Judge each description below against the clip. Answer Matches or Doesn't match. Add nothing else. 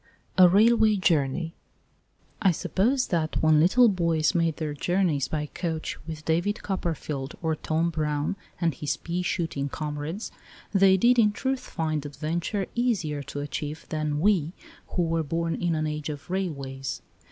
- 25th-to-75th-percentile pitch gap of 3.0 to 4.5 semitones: Matches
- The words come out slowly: Doesn't match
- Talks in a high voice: Doesn't match